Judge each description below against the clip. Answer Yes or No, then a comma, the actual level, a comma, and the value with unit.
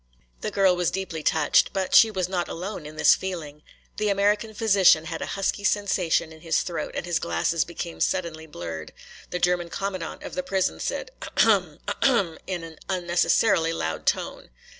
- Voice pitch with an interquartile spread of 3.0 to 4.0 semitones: Yes, average, 3.3 semitones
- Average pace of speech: Yes, average, 180 wpm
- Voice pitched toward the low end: No, medium, 175 Hz